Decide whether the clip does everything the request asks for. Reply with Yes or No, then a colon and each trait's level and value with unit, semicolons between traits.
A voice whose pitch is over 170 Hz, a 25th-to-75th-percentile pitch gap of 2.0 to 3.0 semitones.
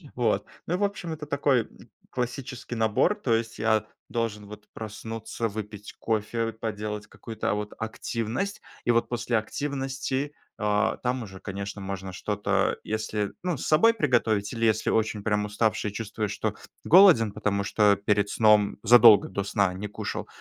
No: low, 110 Hz; average, 2.7 semitones